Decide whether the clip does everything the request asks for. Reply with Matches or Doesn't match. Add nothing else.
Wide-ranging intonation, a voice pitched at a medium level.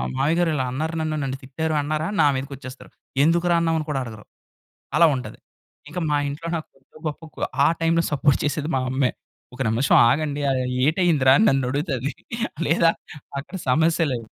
Doesn't match